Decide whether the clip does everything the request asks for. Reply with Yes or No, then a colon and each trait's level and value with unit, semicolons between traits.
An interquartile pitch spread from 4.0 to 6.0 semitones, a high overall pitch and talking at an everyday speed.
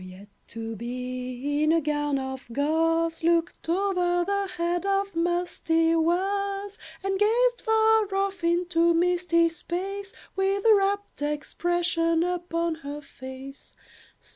No: average, 4.6 semitones; very high, 340 Hz; slow, 125 wpm